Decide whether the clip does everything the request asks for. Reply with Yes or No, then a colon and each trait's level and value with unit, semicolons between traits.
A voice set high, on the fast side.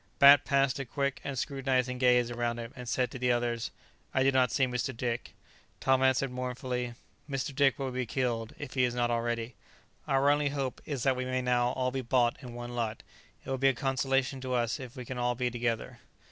No: low, 125 Hz; fast, 225 wpm